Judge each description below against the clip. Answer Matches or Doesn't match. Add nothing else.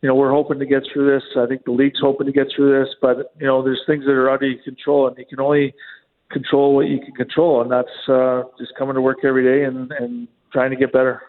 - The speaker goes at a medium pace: Doesn't match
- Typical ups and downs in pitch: Doesn't match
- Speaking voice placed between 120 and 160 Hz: Matches